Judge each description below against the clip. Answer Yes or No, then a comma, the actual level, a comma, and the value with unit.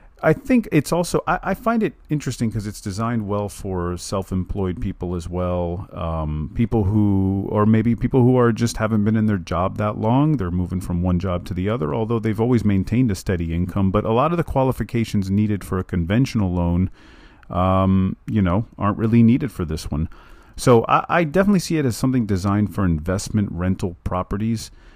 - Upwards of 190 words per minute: Yes, average, 200 wpm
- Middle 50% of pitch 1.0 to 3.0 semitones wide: No, average, 4.2 semitones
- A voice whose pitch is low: Yes, low, 105 Hz